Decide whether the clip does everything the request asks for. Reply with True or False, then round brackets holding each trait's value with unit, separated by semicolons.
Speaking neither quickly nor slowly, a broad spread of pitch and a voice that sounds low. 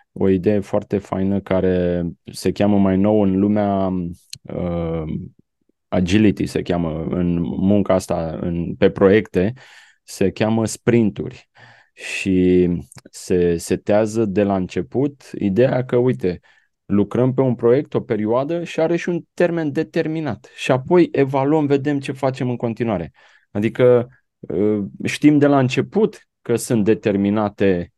True (135 wpm; 5.7 semitones; 105 Hz)